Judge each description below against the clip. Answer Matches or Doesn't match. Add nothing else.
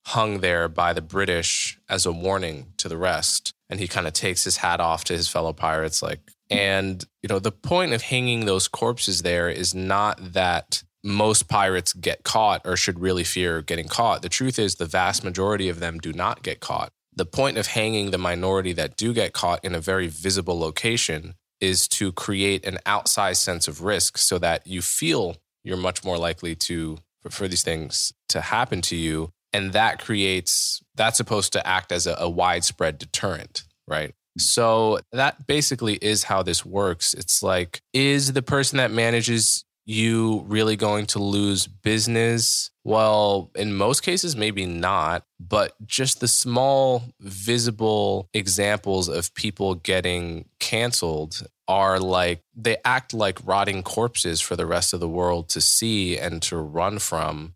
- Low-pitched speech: Matches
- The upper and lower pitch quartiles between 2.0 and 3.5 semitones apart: Doesn't match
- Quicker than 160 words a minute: Matches